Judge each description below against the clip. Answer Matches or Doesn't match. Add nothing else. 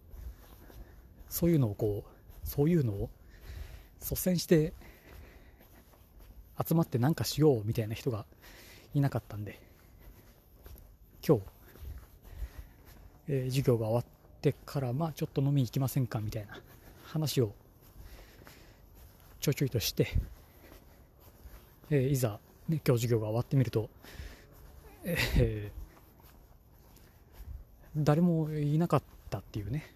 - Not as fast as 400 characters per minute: Matches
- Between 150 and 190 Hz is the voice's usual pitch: Doesn't match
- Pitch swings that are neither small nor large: Doesn't match